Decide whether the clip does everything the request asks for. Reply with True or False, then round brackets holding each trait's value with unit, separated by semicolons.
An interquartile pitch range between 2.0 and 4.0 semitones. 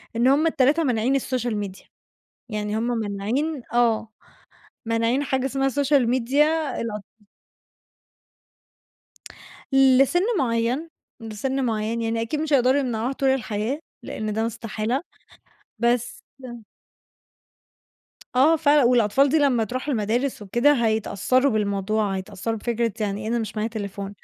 True (3.7 semitones)